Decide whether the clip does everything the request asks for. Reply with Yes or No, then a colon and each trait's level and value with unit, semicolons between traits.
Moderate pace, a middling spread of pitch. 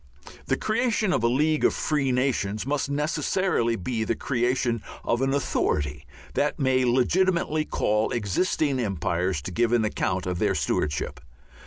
No: average, 150 wpm; wide, 6.2 semitones